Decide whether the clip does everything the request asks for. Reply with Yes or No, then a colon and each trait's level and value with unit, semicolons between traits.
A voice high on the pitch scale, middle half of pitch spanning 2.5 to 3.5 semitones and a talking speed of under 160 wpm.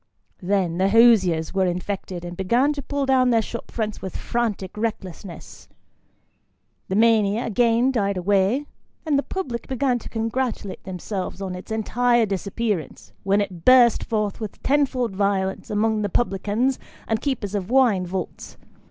No: high, 215 Hz; average, 3.9 semitones; average, 150 wpm